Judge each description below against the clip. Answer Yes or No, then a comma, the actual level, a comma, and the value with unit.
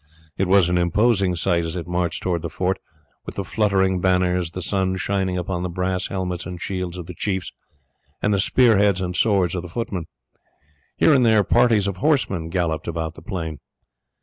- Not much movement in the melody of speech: Yes, narrow, 2.1 semitones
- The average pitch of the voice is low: Yes, very low, 90 Hz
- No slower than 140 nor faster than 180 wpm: No, average, 195 wpm